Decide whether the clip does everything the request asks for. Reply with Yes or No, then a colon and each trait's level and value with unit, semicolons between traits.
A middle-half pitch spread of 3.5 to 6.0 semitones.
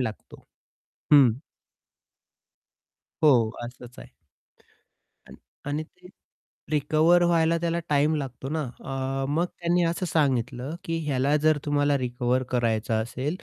Yes: average, 4.1 semitones